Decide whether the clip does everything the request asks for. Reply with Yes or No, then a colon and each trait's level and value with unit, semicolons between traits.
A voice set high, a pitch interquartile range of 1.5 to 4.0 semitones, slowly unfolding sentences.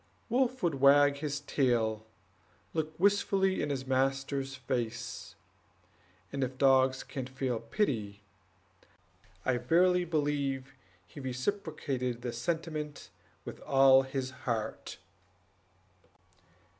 No: low, 135 Hz; average, 3.0 semitones; slow, 100 wpm